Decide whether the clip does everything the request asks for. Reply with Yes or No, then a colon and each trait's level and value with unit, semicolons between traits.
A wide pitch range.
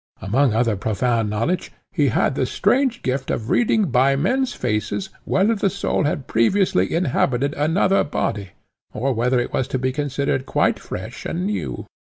Yes: wide, 7.9 semitones